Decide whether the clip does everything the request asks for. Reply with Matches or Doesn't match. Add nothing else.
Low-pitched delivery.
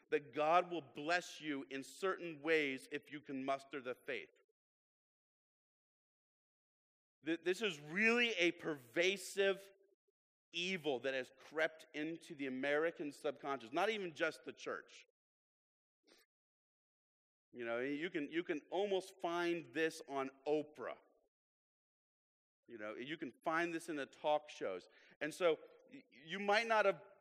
Doesn't match